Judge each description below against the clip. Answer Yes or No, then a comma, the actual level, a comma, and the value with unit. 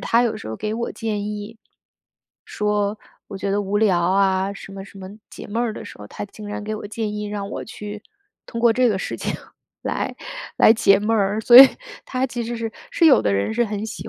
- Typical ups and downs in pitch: No, narrow, 2.3 semitones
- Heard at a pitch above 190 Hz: Yes, high, 210 Hz